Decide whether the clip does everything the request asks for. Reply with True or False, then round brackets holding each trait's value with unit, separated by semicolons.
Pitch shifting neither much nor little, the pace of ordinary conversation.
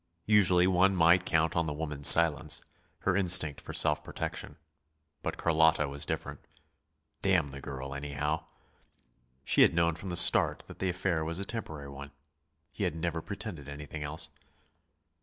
True (3.3 semitones; 160 wpm)